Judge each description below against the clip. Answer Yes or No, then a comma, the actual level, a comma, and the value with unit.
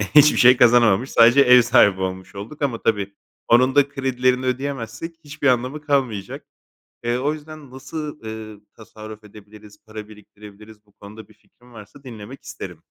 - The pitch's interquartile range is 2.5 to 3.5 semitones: No, average, 4.0 semitones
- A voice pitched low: Yes, low, 120 Hz